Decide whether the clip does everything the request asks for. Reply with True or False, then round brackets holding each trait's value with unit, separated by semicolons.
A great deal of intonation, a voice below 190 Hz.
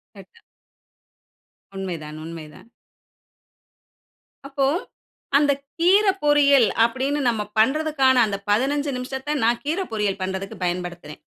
False (7.0 semitones; 250 Hz)